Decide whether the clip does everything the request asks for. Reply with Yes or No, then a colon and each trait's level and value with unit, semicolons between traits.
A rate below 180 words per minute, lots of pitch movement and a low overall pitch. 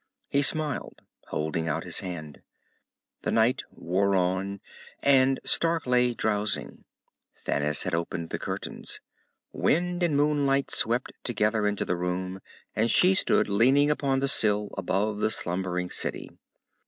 Yes: slow, 135 wpm; wide, 6.9 semitones; low, 105 Hz